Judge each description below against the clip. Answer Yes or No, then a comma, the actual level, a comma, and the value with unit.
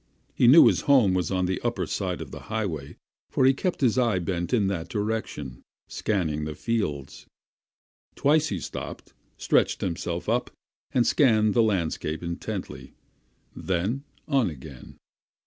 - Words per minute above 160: No, average, 145 wpm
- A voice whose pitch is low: Yes, low, 100 Hz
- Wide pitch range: Yes, wide, 6.0 semitones